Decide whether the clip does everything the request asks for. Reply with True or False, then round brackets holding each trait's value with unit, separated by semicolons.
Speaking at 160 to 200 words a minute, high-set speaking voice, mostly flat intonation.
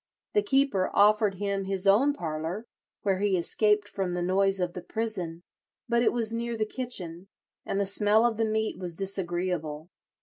False (175 wpm; 195 Hz; 3.4 semitones)